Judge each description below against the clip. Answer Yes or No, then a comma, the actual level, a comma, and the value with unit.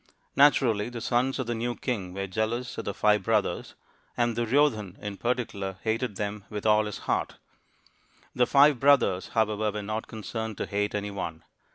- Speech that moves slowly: No, average, 165 wpm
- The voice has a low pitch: Yes, low, 110 Hz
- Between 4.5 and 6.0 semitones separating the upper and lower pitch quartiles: No, average, 2.8 semitones